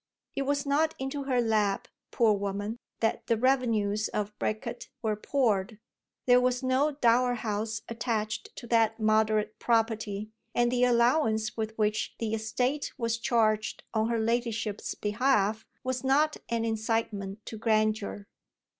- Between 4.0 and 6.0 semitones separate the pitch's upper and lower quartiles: No, narrow, 2.4 semitones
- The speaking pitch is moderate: No, high, 225 Hz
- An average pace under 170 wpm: Yes, average, 140 wpm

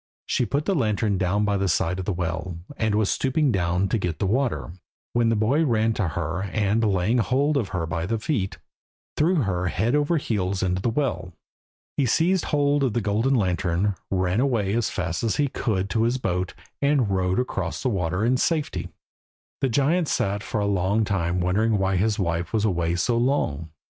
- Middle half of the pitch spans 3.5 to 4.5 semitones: No, average, 5.2 semitones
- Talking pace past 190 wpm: Yes, average, 200 wpm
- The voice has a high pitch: No, low, 105 Hz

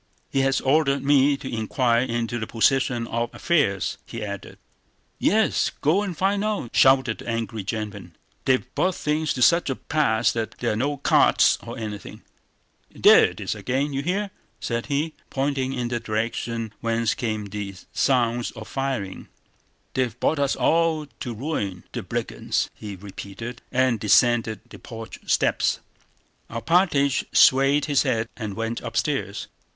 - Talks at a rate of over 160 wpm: No, average, 155 wpm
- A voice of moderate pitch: No, low, 120 Hz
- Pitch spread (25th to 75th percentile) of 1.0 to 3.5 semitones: No, average, 4.0 semitones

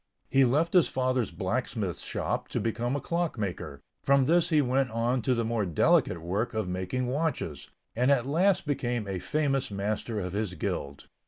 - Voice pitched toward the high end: No, low, 120 Hz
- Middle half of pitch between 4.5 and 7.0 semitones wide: Yes, wide, 5.5 semitones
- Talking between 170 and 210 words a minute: Yes, average, 180 wpm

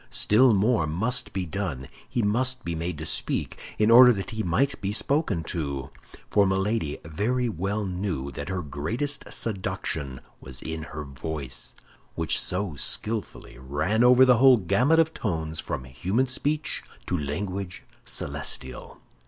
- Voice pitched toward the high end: No, very low, 95 Hz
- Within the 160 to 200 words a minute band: No, average, 145 wpm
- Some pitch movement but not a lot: No, wide, 6.9 semitones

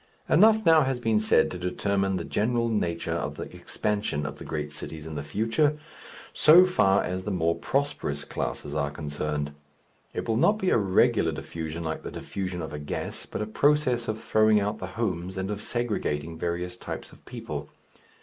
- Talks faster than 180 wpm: Yes, average, 190 wpm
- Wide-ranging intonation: Yes, wide, 6.3 semitones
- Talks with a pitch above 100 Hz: No, very low, 95 Hz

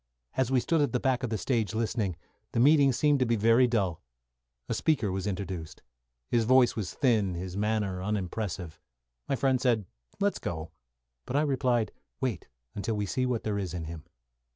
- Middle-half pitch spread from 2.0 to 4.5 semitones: No, average, 5.2 semitones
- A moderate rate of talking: Yes, average, 185 wpm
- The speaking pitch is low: Yes, low, 110 Hz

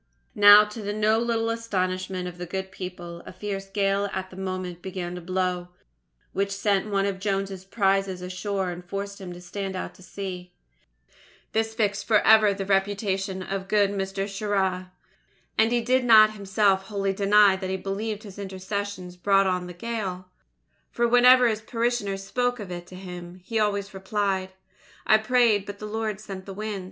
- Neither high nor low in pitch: No, high, 195 Hz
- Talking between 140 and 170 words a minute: No, average, 180 wpm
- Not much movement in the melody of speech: Yes, narrow, 2.1 semitones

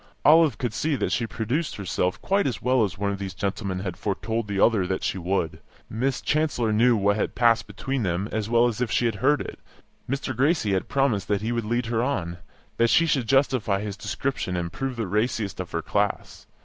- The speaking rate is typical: No, fast, 220 wpm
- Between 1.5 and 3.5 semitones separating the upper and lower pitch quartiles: No, average, 4.4 semitones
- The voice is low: Yes, low, 110 Hz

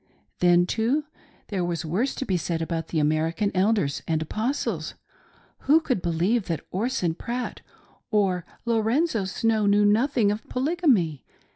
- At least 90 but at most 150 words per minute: Yes, average, 145 wpm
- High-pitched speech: Yes, high, 205 Hz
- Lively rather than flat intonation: Yes, wide, 5.8 semitones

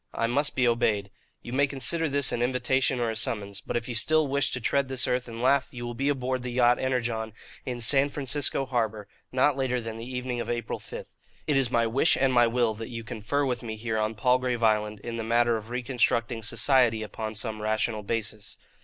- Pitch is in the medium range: No, low, 120 Hz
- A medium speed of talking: No, fast, 220 wpm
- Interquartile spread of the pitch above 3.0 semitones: No, narrow, 2.5 semitones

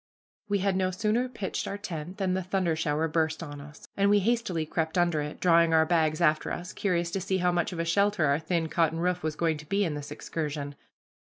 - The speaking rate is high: Yes, fast, 235 wpm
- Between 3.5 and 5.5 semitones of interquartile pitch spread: No, average, 3.1 semitones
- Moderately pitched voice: Yes, medium, 170 Hz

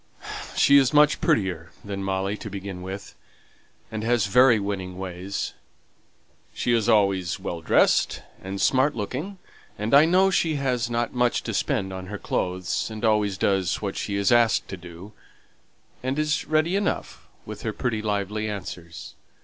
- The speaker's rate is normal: Yes, average, 150 wpm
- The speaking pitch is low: Yes, low, 105 Hz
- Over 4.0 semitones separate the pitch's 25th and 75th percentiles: Yes, average, 4.5 semitones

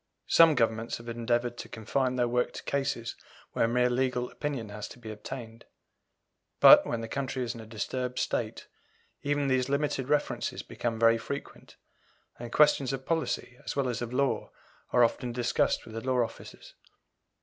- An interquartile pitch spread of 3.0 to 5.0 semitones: No, narrow, 2.6 semitones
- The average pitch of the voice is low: Yes, low, 125 Hz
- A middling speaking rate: Yes, average, 175 wpm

